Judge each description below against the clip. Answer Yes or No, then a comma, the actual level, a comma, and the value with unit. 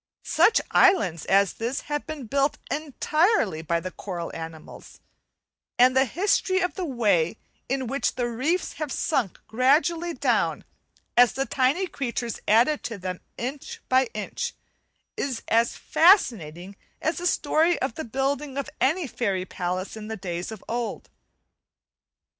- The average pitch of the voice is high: Yes, very high, 255 Hz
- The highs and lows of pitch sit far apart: Yes, wide, 7.0 semitones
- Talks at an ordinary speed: Yes, average, 145 wpm